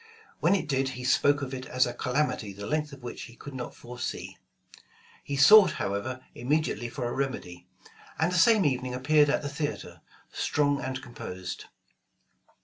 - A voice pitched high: No, low, 135 Hz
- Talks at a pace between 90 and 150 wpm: No, average, 170 wpm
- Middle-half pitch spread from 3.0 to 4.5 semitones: Yes, average, 3.3 semitones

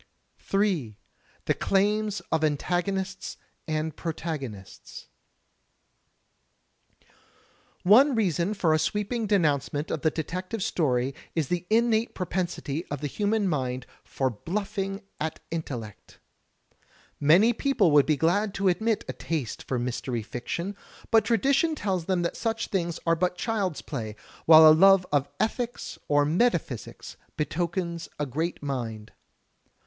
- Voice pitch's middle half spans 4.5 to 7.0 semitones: Yes, wide, 5.5 semitones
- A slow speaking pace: Yes, slow, 125 wpm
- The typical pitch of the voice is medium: Yes, medium, 170 Hz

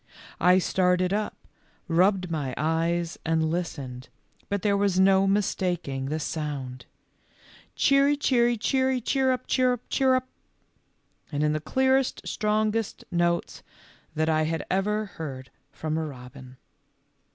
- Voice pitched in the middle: Yes, medium, 180 Hz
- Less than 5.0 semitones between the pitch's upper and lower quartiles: No, wide, 5.4 semitones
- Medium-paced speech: No, slow, 120 wpm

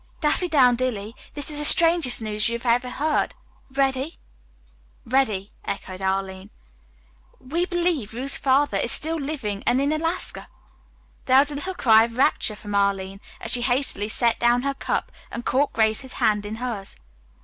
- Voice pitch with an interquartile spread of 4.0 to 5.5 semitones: Yes, average, 5.2 semitones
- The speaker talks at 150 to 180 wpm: Yes, average, 155 wpm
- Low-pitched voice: No, very high, 250 Hz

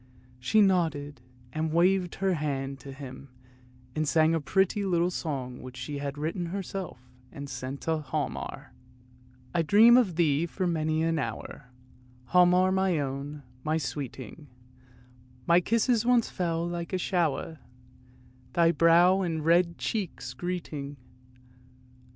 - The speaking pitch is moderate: Yes, medium, 165 Hz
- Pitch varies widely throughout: No, average, 4.1 semitones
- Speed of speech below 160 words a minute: Yes, slow, 135 wpm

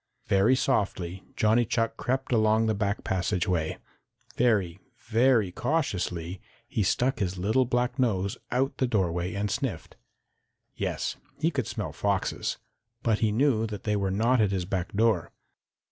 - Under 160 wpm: Yes, average, 145 wpm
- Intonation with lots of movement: No, average, 4.2 semitones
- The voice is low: Yes, low, 105 Hz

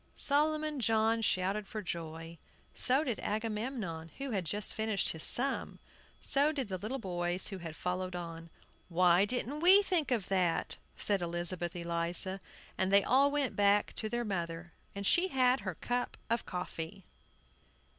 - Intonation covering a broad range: Yes, wide, 6.2 semitones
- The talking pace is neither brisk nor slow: Yes, average, 155 wpm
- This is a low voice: No, high, 200 Hz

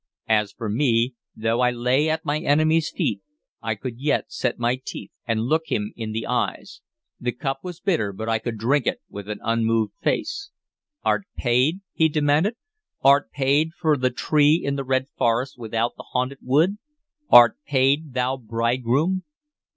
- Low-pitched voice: Yes, low, 130 Hz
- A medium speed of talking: Yes, average, 170 wpm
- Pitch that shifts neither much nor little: Yes, average, 4.4 semitones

